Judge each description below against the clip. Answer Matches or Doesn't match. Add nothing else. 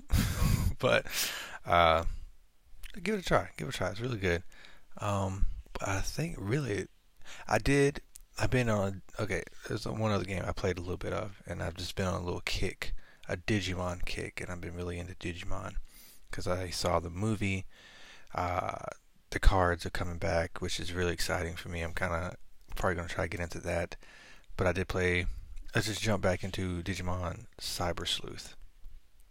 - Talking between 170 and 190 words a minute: Matches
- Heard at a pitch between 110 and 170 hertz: Doesn't match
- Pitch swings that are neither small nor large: Doesn't match